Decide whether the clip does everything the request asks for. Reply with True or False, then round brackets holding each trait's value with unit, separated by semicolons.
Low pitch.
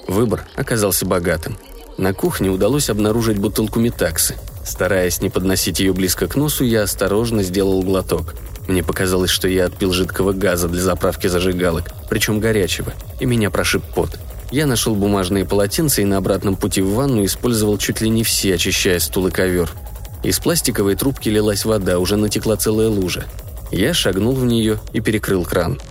True (100 Hz)